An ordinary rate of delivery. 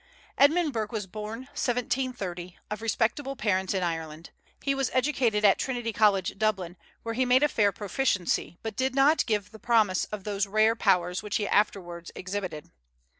Yes: average, 165 wpm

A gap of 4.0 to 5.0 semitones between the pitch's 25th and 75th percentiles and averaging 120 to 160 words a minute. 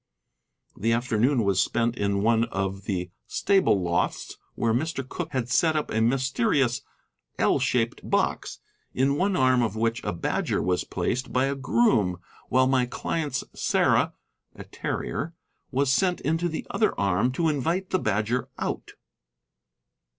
Yes: average, 4.4 semitones; average, 150 wpm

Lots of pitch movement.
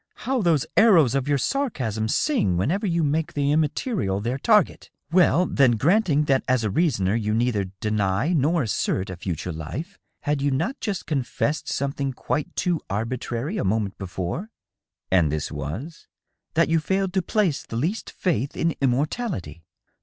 Yes: wide, 8.1 semitones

